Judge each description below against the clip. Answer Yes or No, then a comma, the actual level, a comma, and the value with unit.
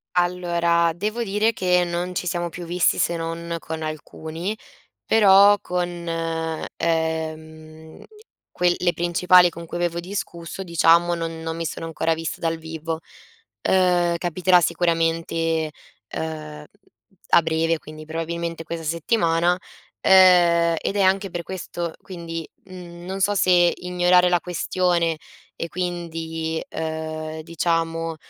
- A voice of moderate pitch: Yes, medium, 170 Hz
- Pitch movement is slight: Yes, narrow, 1.5 semitones